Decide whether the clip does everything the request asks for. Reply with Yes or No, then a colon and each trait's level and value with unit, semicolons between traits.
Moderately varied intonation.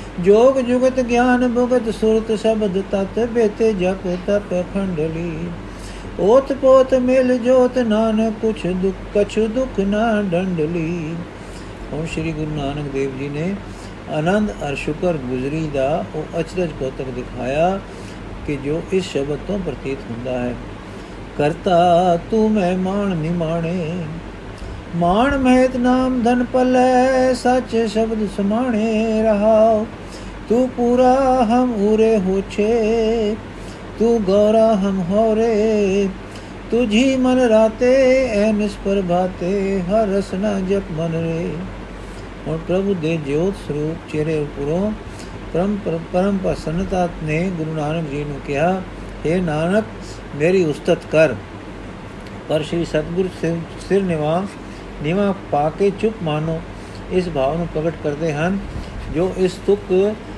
No: wide, 6.2 semitones